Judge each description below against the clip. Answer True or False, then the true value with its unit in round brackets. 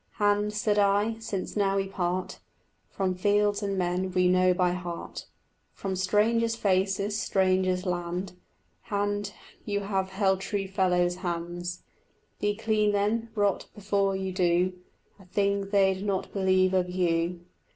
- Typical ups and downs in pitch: False (1.9 semitones)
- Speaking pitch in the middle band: False (195 Hz)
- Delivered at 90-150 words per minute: True (140 wpm)